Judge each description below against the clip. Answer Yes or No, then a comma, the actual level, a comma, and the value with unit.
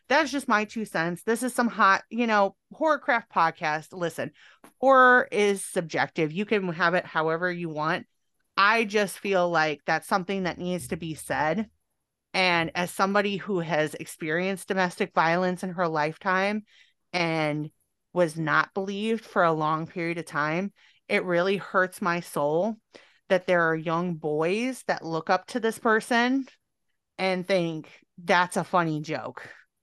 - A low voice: No, medium, 180 Hz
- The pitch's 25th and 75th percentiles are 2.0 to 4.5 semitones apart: Yes, average, 4.0 semitones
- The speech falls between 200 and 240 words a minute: No, average, 155 wpm